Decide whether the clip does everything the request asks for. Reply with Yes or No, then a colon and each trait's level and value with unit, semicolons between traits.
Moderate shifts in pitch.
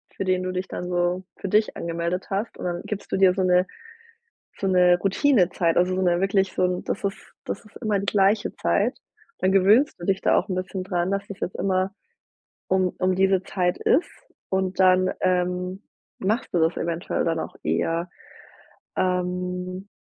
No: narrow, 1.3 semitones